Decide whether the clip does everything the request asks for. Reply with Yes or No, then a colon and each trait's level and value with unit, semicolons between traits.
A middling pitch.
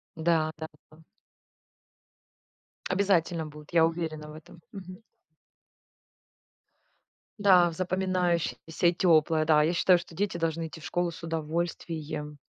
Yes: medium, 165 Hz